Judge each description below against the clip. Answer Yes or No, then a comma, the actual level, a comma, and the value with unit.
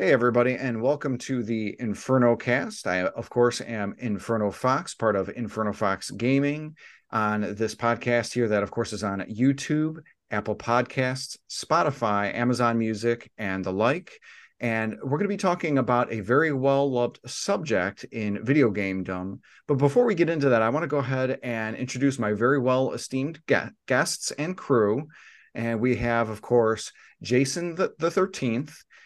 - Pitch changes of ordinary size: Yes, average, 3.8 semitones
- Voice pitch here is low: Yes, low, 120 Hz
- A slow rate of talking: No, average, 165 wpm